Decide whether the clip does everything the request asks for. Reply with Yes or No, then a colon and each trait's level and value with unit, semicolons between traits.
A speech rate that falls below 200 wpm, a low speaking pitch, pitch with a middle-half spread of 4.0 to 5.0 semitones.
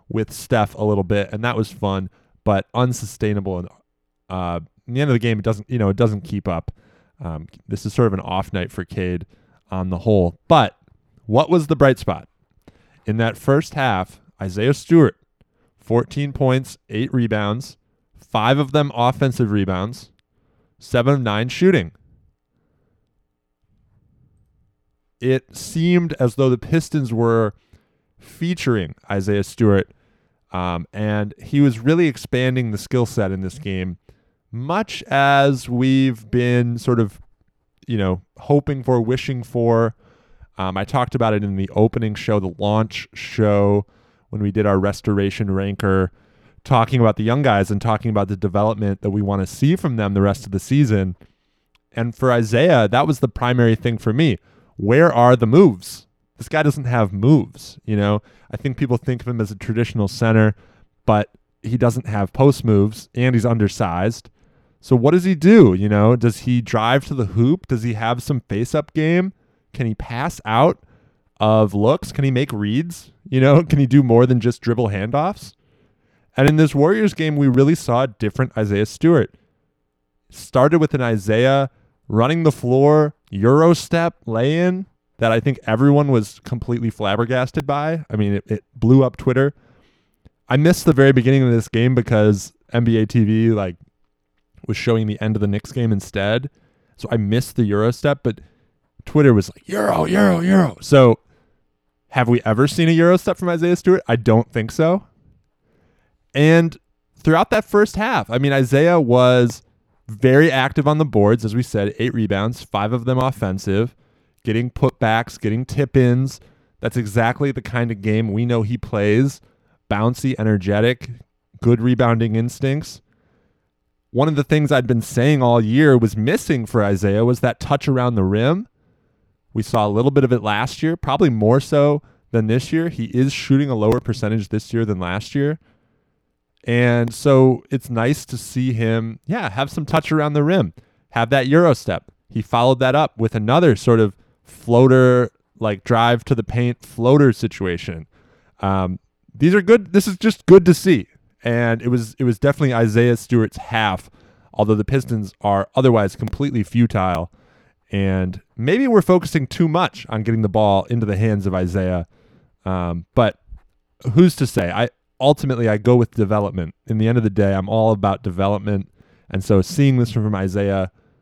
Yes: average, 170 wpm; low, 120 Hz; average, 4.5 semitones